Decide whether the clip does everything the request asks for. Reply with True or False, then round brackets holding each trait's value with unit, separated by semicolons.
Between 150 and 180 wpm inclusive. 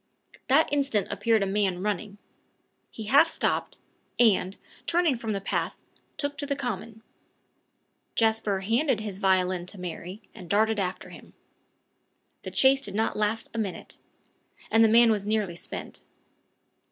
False (140 wpm)